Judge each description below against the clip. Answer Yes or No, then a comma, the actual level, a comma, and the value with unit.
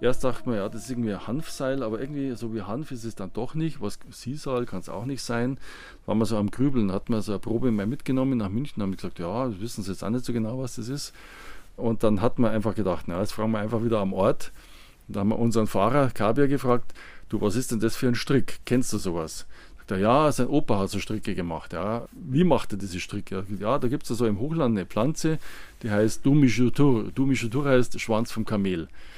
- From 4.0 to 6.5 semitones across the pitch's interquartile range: No, average, 3.4 semitones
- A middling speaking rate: No, fast, 245 wpm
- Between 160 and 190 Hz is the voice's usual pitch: No, low, 115 Hz